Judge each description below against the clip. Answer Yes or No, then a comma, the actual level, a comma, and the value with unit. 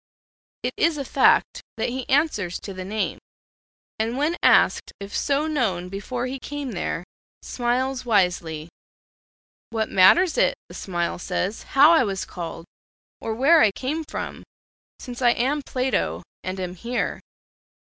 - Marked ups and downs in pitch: Yes, wide, 6.3 semitones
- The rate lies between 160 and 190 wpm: No, average, 145 wpm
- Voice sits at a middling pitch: No, high, 240 Hz